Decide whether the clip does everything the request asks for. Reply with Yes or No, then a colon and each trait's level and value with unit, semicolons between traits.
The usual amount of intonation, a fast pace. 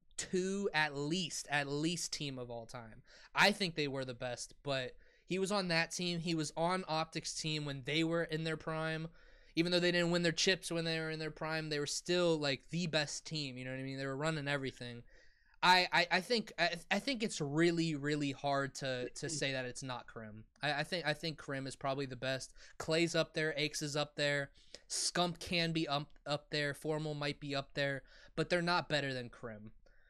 Yes: average, 3.3 semitones; fast, 225 wpm